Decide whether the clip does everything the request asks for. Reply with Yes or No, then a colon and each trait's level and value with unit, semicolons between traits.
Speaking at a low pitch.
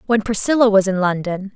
No: high, 205 Hz